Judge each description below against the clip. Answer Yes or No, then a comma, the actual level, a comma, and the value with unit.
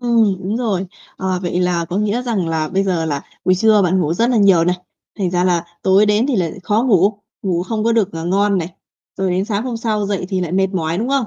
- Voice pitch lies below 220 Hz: Yes, high, 195 Hz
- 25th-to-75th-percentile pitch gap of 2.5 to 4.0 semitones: Yes, average, 3.3 semitones